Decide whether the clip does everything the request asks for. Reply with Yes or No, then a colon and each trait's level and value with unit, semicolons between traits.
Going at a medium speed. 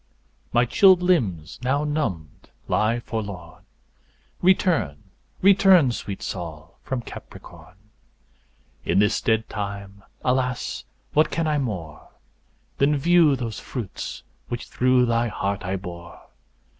No: slow, 115 wpm